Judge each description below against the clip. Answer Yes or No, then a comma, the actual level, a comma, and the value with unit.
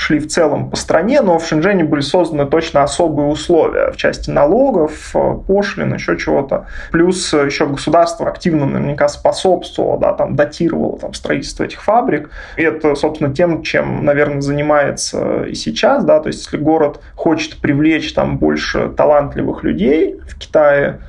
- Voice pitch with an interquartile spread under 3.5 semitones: Yes, average, 2.8 semitones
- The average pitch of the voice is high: No, medium, 155 Hz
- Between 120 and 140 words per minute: No, average, 155 wpm